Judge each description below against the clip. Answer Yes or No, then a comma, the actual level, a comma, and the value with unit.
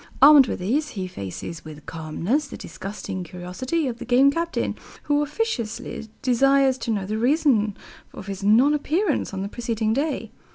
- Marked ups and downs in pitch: Yes, wide, 6.5 semitones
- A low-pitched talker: No, high, 240 Hz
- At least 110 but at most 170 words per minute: Yes, average, 165 wpm